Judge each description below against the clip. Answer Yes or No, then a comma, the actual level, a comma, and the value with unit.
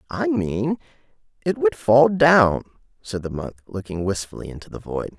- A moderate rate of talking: Yes, average, 160 wpm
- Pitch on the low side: Yes, low, 110 Hz